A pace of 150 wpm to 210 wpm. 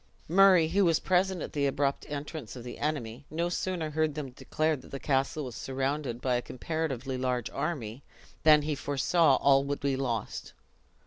Yes: average, 180 wpm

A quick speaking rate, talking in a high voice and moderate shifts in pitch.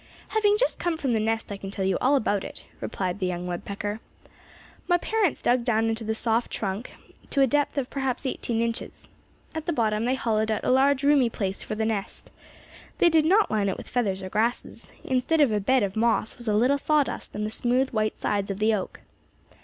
Yes: fast, 220 wpm; high, 230 Hz; average, 4.4 semitones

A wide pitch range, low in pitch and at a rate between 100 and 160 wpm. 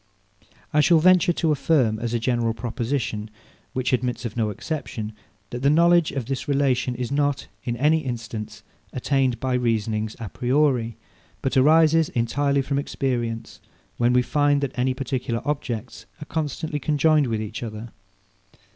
No: average, 3.8 semitones; low, 130 Hz; average, 155 wpm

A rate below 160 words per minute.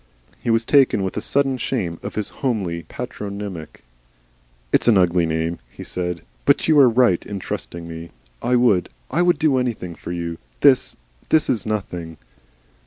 No: average, 165 wpm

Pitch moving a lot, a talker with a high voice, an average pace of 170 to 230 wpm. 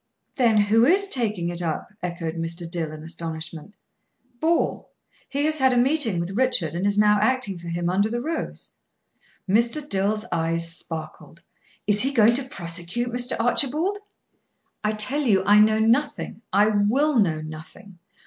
No: wide, 6.4 semitones; high, 210 Hz; average, 160 wpm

